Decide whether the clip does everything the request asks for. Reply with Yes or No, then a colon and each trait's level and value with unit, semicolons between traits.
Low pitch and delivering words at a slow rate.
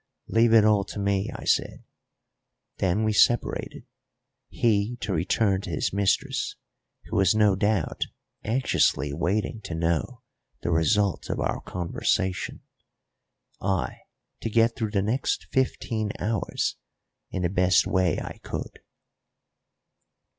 Yes: low, 100 Hz; slow, 125 wpm